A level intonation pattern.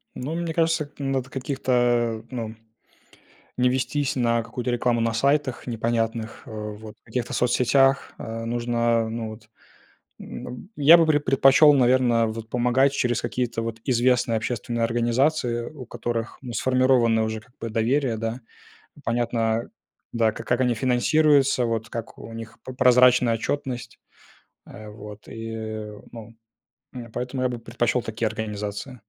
Yes: narrow, 2.2 semitones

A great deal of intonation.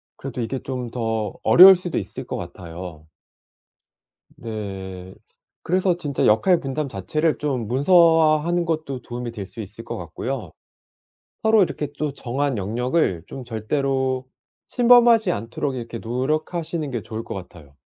Yes: wide, 6.1 semitones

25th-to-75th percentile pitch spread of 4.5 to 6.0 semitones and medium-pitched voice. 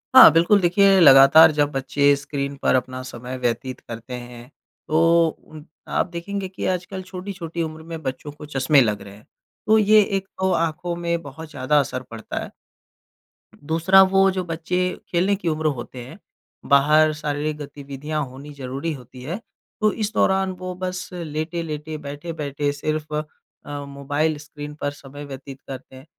No: average, 3.8 semitones; medium, 150 Hz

